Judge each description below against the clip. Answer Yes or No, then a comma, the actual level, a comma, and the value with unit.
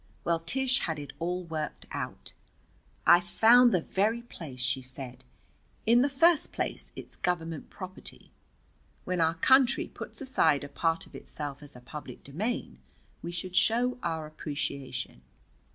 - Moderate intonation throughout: No, wide, 7.6 semitones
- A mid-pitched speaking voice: Yes, medium, 170 Hz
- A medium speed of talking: Yes, average, 150 wpm